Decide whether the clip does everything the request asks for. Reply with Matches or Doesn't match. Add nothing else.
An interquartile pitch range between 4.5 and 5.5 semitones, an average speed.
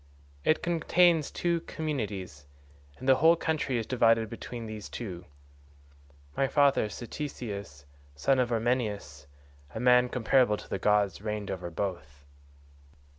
Doesn't match